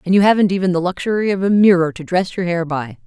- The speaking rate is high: Yes, fast, 275 wpm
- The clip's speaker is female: Yes, female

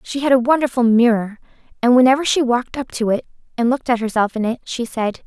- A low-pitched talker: No, high, 240 Hz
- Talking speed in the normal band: No, fast, 230 wpm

